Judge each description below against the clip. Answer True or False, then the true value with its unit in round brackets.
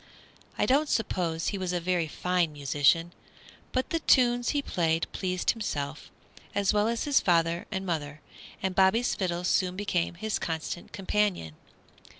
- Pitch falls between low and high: True (180 Hz)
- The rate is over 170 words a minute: False (155 wpm)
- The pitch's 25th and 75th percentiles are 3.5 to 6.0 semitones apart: True (4.0 semitones)